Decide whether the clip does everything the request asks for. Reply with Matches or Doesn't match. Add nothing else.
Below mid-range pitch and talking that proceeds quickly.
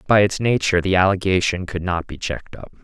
Matches